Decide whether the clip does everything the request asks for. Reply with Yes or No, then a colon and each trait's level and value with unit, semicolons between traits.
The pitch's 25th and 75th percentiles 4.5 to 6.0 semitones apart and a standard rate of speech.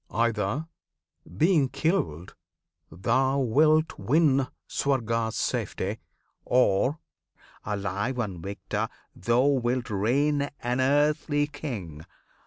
No: wide, 5.6 semitones; slow, 85 wpm